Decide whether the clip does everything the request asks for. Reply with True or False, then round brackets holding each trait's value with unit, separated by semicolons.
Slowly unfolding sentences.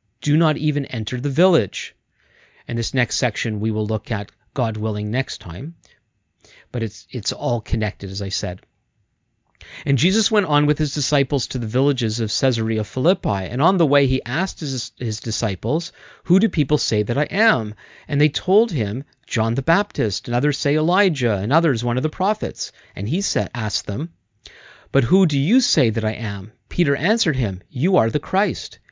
False (190 wpm)